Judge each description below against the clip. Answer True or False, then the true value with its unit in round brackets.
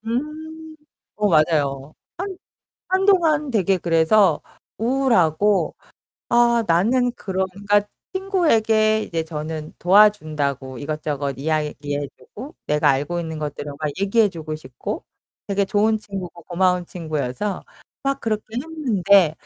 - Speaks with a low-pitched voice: False (190 Hz)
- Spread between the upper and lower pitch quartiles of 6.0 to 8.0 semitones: True (6.8 semitones)